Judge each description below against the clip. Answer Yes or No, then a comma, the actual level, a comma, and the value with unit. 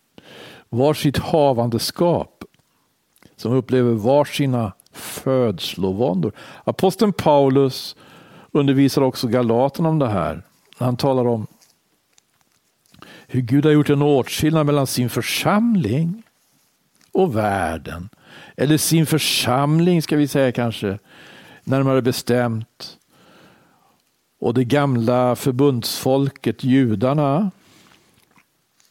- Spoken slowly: Yes, slow, 85 wpm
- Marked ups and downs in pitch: No, average, 3.1 semitones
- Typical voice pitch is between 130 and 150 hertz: Yes, low, 135 Hz